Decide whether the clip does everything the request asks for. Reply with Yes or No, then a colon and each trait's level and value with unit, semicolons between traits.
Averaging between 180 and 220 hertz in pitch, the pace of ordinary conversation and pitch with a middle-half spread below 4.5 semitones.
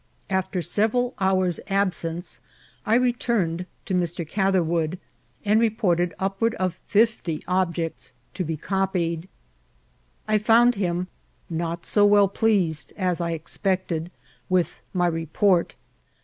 No: medium, 185 Hz; slow, 115 wpm; average, 3.3 semitones